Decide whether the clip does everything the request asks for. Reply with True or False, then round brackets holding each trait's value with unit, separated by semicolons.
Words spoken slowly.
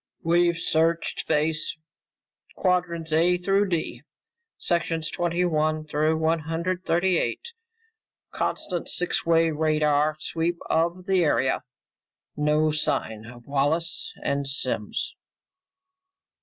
True (105 wpm)